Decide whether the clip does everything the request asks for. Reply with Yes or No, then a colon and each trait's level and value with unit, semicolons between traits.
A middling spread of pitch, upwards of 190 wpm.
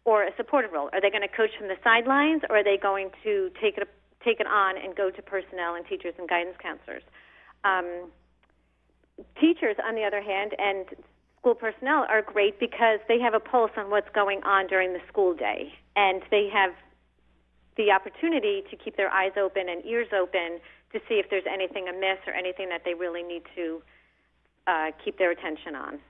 Yes: average, 3.5 semitones; average, 200 wpm